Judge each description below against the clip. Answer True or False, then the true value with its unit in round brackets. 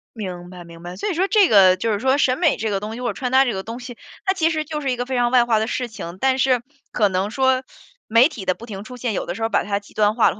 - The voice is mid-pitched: False (230 Hz)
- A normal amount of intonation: True (4.5 semitones)